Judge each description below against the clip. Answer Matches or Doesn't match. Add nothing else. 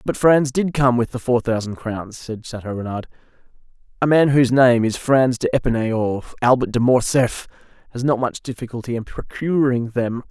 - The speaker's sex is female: Doesn't match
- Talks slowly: Doesn't match